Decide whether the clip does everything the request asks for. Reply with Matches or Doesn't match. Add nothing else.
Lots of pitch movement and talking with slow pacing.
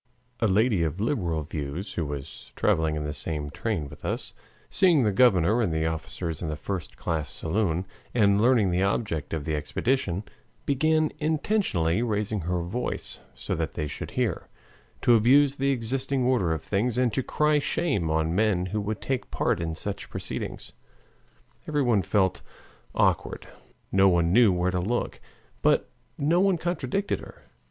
Doesn't match